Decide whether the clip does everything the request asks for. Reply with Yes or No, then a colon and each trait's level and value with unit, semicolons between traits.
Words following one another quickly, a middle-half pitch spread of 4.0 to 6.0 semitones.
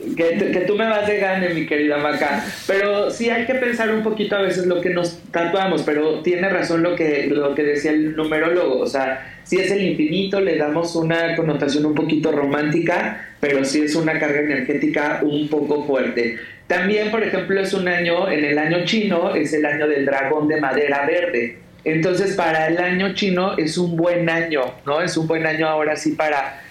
No: fast, 200 wpm; average, 3.4 semitones